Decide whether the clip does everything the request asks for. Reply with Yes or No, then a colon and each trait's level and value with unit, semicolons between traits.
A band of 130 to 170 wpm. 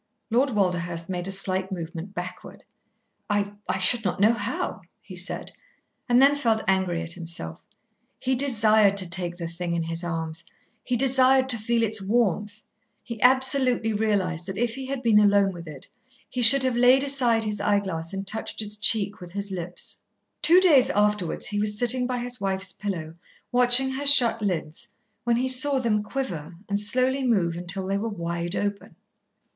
No: average, 180 wpm